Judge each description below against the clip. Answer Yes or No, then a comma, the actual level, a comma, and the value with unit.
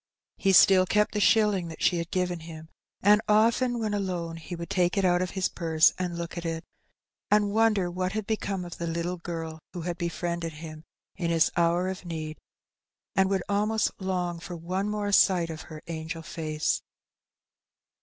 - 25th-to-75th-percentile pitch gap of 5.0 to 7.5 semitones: No, average, 2.8 semitones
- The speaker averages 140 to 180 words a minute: No, average, 190 wpm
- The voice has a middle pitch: Yes, medium, 175 Hz